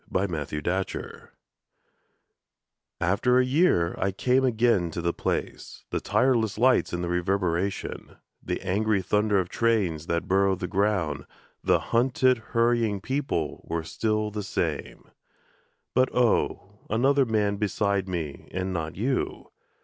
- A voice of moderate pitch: No, low, 100 Hz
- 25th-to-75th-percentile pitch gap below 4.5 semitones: No, average, 4.8 semitones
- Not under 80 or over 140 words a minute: Yes, slow, 135 wpm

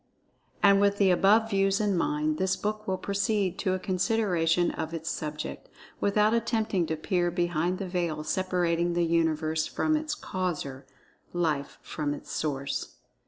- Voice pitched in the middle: Yes, medium, 180 Hz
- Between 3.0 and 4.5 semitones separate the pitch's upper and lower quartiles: Yes, average, 3.8 semitones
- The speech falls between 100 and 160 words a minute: Yes, average, 150 wpm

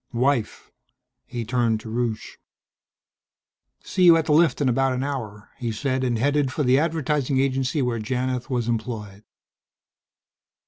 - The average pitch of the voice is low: Yes, low, 130 Hz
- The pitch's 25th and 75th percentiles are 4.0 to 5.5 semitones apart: No, average, 3.2 semitones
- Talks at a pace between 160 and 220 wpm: No, average, 145 wpm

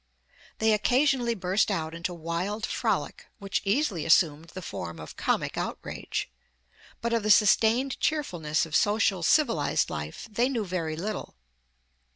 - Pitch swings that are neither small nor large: No, wide, 5.7 semitones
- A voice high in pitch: Yes, high, 195 Hz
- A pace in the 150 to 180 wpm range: No, average, 140 wpm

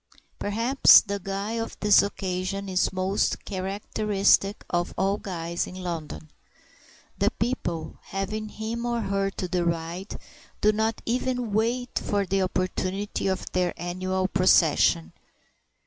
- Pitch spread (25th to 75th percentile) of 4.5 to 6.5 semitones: No, narrow, 2.6 semitones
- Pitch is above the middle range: Yes, high, 195 Hz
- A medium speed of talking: No, slow, 125 wpm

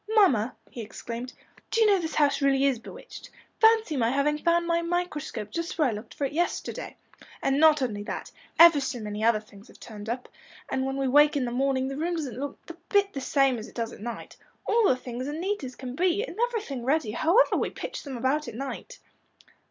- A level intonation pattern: No, wide, 5.6 semitones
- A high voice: Yes, very high, 275 Hz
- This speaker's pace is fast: Yes, fast, 230 wpm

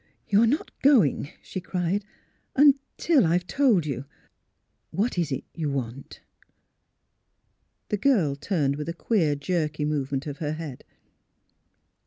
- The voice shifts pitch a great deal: Yes, wide, 6.4 semitones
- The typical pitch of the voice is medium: Yes, medium, 165 Hz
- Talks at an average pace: Yes, average, 150 wpm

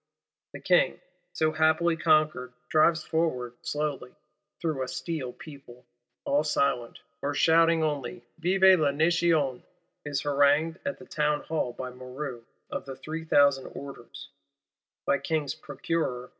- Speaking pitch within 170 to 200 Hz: No, medium, 150 Hz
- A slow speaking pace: Yes, slow, 130 wpm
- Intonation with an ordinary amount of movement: Yes, average, 3.2 semitones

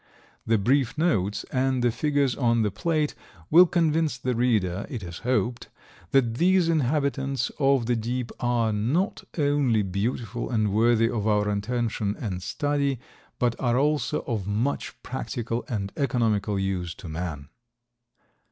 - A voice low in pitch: Yes, low, 120 Hz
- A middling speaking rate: Yes, average, 145 wpm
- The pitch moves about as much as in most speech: Yes, average, 4.8 semitones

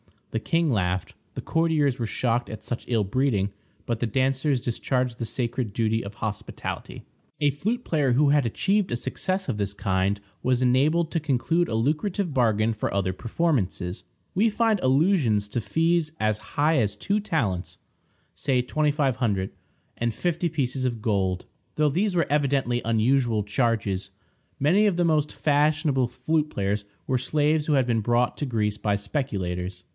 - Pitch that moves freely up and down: Yes, wide, 6.0 semitones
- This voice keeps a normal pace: Yes, average, 160 wpm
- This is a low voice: Yes, low, 125 Hz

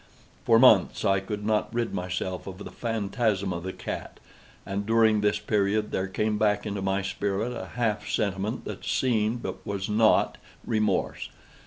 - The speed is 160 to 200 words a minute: Yes, average, 165 wpm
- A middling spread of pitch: No, narrow, 2.2 semitones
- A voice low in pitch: Yes, low, 105 Hz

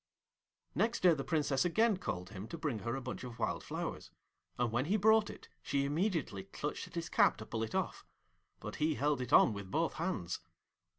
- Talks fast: Yes, fast, 210 wpm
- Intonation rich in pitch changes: Yes, wide, 6.7 semitones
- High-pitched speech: No, medium, 140 Hz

